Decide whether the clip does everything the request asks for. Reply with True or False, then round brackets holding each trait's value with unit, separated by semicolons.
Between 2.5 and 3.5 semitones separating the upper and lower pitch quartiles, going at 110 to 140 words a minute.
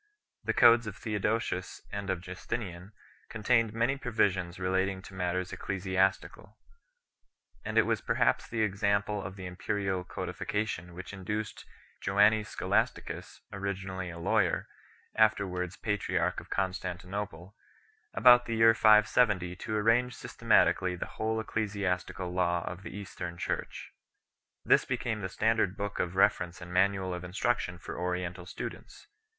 True (2.9 semitones; 135 wpm)